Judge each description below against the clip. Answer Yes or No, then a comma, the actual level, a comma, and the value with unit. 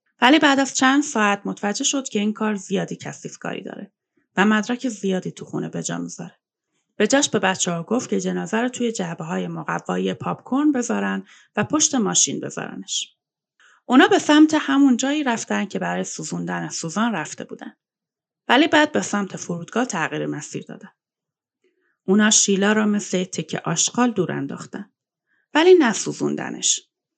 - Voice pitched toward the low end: No, high, 210 Hz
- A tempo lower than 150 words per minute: No, fast, 155 wpm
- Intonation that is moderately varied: No, wide, 7.3 semitones